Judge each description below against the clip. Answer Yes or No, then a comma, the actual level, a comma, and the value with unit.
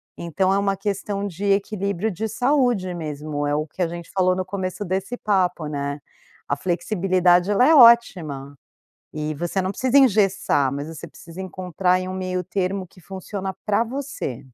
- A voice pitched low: No, medium, 185 Hz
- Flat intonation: No, average, 3.1 semitones